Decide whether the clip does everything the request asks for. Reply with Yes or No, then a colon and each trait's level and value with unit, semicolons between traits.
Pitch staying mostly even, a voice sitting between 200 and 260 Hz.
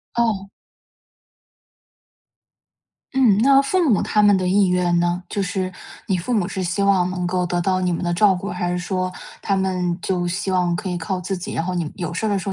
No: narrow, 2.0 semitones; medium, 185 Hz